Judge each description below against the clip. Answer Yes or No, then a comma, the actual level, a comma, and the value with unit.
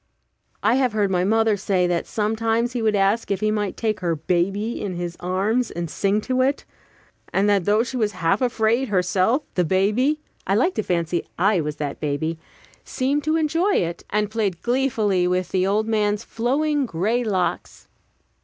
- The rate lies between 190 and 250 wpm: No, average, 180 wpm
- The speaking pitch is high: Yes, high, 210 Hz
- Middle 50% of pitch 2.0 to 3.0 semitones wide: No, average, 4.2 semitones